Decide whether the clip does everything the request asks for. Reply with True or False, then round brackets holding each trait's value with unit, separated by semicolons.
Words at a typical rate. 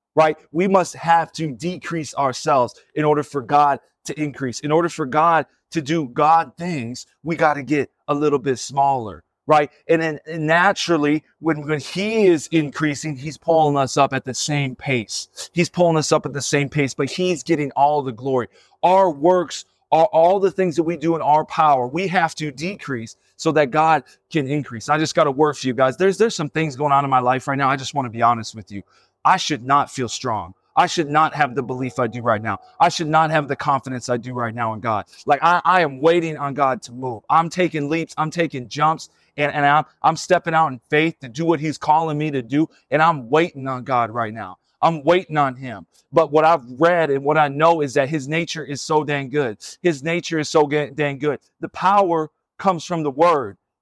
False (230 wpm)